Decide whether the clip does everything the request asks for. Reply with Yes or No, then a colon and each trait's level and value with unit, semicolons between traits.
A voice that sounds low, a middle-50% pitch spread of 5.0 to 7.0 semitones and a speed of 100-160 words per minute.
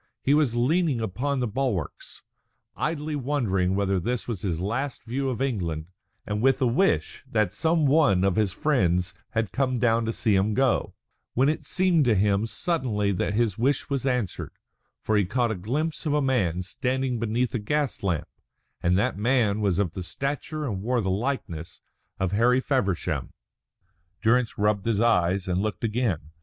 No: low, 115 Hz; average, 5.3 semitones; average, 175 wpm